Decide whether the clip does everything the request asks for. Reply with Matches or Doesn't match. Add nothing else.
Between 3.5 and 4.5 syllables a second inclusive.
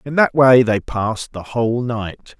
Matches